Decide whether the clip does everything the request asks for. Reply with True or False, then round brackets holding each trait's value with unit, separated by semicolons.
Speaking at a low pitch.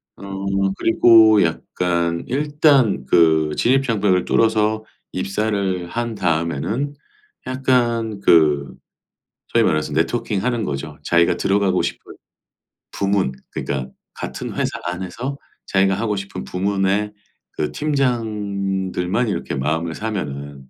True (100 Hz)